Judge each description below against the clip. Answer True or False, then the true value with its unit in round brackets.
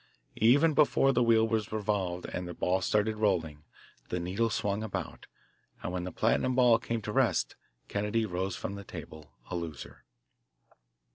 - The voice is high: False (105 Hz)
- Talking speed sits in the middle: True (160 wpm)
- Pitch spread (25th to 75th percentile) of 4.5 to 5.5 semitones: False (4.1 semitones)